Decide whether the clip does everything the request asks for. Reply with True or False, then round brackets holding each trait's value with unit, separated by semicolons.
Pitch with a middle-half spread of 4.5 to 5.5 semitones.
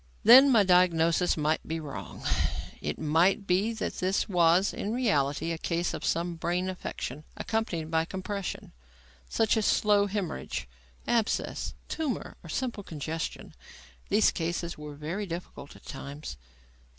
False (4.1 semitones)